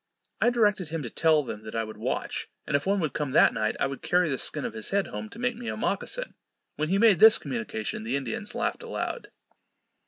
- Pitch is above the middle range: No, medium, 155 Hz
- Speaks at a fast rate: Yes, fast, 240 wpm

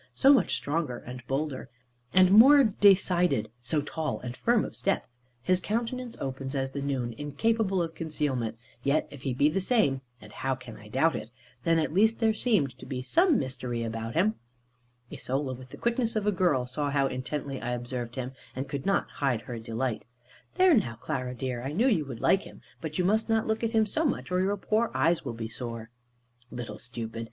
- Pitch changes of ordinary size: No, wide, 7.9 semitones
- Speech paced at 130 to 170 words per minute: No, fast, 205 wpm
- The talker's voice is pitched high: No, medium, 145 Hz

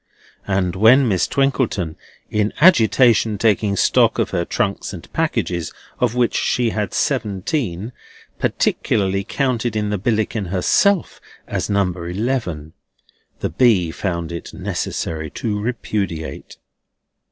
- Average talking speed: No, slow, 120 wpm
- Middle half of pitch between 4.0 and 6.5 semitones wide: Yes, average, 4.8 semitones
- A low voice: Yes, low, 105 Hz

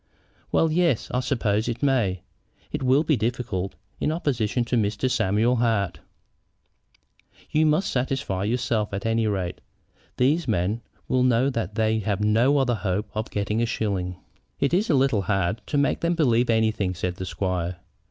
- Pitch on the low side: Yes, low, 115 Hz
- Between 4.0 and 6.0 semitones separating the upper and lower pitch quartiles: Yes, average, 4.5 semitones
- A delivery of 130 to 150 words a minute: No, average, 165 wpm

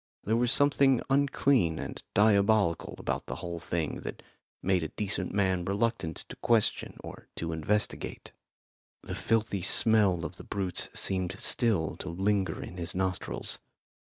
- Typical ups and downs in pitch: Yes, average, 4.1 semitones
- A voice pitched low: Yes, very low, 95 Hz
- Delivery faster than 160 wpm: No, average, 145 wpm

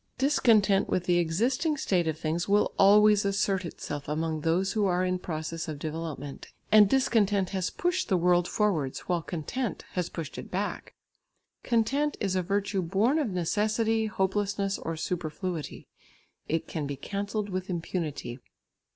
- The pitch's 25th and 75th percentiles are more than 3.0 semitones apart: Yes, average, 4.1 semitones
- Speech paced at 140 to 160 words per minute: Yes, average, 150 wpm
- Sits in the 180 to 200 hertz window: Yes, high, 190 Hz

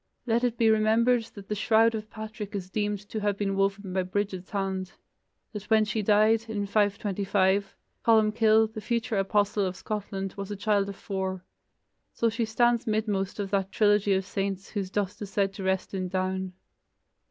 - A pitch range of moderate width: No, narrow, 2.0 semitones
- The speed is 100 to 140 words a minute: No, average, 180 wpm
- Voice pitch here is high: Yes, high, 205 Hz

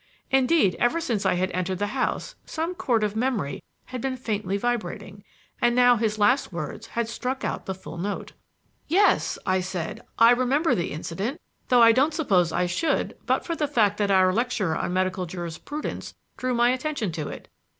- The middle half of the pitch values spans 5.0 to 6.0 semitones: Yes, wide, 5.4 semitones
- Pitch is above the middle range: Yes, high, 225 Hz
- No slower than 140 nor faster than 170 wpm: No, average, 185 wpm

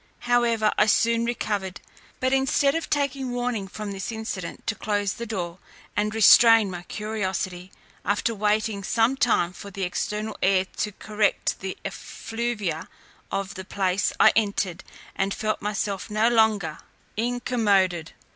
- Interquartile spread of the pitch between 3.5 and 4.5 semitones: No, average, 3.0 semitones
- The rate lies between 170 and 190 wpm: No, average, 140 wpm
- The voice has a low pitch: No, high, 210 Hz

